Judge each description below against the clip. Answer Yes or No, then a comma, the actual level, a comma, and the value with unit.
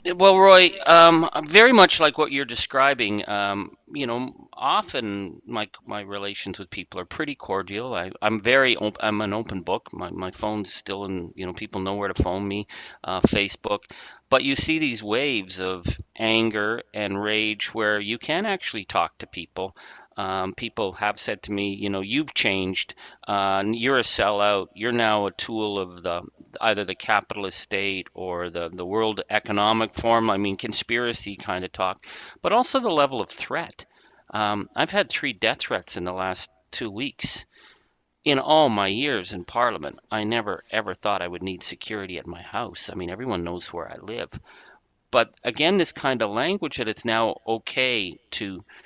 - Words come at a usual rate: Yes, average, 180 wpm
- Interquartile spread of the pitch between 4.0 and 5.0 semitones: No, average, 3.3 semitones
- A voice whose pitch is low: Yes, low, 105 Hz